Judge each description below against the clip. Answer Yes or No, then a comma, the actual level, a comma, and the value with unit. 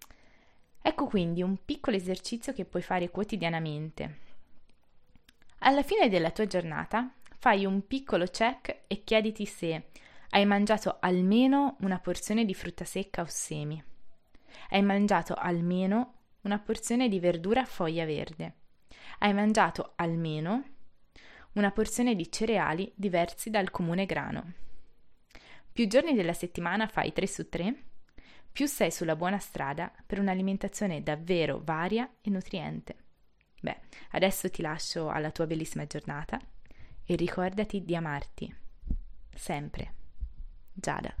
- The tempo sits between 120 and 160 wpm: Yes, average, 125 wpm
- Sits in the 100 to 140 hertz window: No, medium, 185 Hz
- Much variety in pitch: No, average, 4.7 semitones